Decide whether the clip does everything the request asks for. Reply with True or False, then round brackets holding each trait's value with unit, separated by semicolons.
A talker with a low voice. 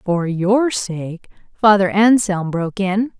False (200 Hz)